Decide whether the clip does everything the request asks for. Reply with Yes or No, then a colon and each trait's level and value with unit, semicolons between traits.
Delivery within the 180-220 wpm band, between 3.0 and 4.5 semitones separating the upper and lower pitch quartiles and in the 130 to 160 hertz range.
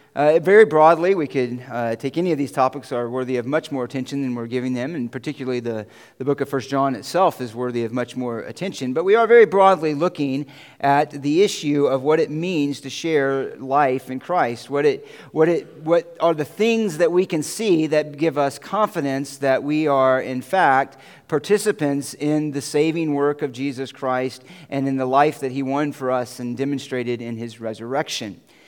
Yes: fast, 205 wpm; average, 3.6 semitones; medium, 140 Hz